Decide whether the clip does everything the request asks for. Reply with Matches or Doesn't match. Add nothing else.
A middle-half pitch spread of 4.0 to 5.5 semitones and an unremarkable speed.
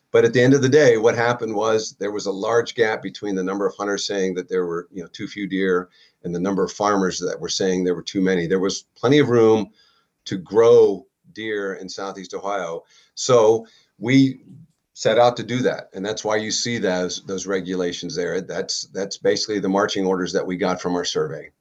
Doesn't match